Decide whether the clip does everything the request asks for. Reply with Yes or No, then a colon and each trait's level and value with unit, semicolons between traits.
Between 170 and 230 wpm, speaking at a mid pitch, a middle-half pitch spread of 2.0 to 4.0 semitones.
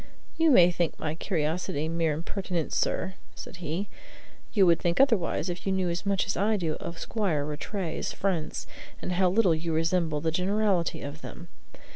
Yes: average, 175 wpm; medium, 175 Hz; average, 3.1 semitones